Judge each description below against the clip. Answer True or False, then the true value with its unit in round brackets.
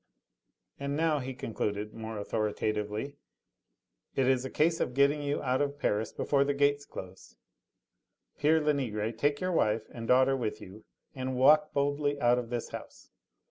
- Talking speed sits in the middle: True (155 wpm)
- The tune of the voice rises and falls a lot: False (4.3 semitones)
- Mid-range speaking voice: False (130 Hz)